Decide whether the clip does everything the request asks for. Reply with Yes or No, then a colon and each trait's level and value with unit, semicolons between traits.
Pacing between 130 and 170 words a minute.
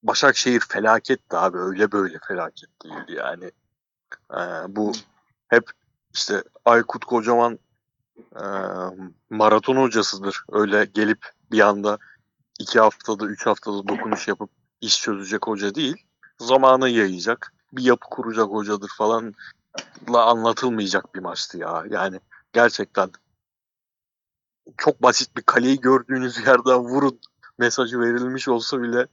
No: average, 115 wpm